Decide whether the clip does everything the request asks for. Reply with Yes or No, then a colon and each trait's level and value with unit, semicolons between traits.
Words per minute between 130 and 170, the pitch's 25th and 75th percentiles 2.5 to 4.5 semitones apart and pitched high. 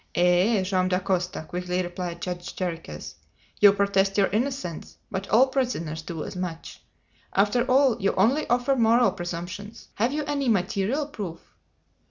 No: average, 145 wpm; average, 5.1 semitones; high, 195 Hz